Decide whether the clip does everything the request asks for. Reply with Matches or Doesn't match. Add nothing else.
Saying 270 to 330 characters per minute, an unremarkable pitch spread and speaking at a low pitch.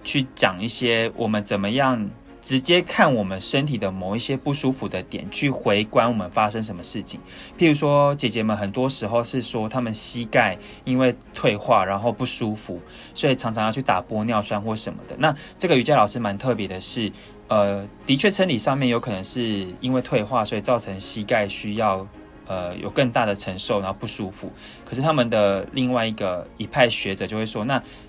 Matches